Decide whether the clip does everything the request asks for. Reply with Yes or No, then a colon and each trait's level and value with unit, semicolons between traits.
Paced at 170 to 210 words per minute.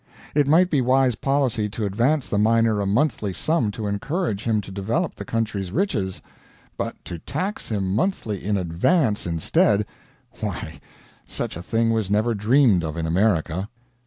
No: average, 160 wpm